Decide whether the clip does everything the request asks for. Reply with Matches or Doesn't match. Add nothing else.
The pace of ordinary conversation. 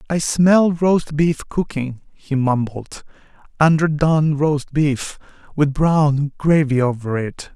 Doesn't match